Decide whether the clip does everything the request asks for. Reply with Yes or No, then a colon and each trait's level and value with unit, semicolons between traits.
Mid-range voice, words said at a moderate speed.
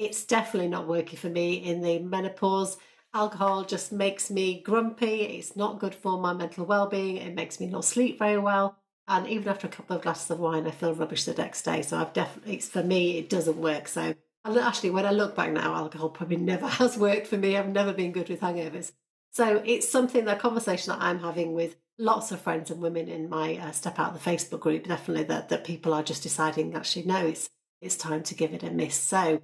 No: medium, 180 Hz; fast, 230 wpm